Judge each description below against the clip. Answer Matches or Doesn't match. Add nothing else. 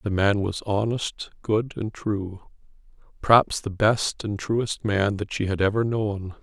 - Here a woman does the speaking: Doesn't match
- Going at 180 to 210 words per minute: Doesn't match